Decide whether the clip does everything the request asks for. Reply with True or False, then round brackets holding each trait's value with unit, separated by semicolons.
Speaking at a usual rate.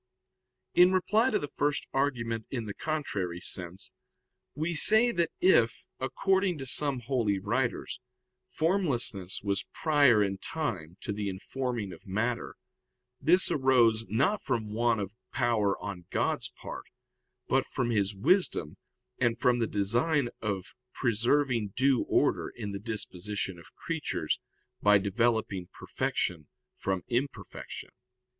False (130 wpm)